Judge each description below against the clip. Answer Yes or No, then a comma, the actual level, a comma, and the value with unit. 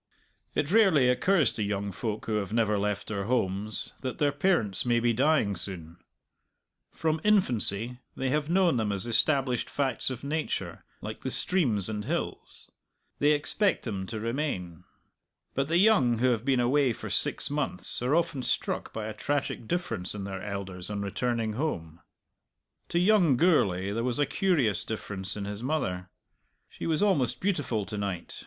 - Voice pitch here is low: Yes, low, 120 Hz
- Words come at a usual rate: Yes, average, 170 wpm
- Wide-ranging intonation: Yes, wide, 6.5 semitones